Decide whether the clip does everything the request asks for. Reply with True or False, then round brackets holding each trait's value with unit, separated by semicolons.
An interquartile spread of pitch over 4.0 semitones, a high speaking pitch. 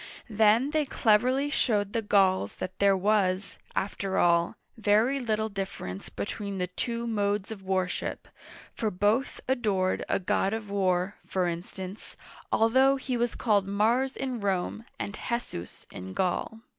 False (3.5 semitones; 205 Hz)